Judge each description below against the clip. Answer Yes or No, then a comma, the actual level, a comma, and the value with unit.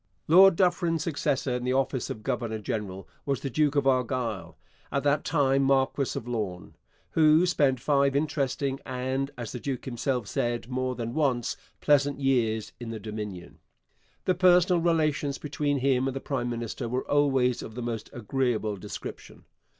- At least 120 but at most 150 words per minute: No, average, 165 wpm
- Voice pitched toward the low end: Yes, low, 130 Hz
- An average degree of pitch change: Yes, average, 3.4 semitones